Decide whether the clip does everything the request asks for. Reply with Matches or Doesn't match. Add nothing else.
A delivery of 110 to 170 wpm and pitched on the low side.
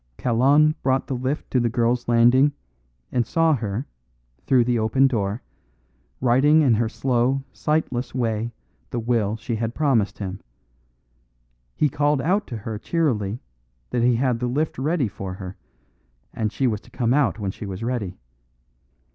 Matches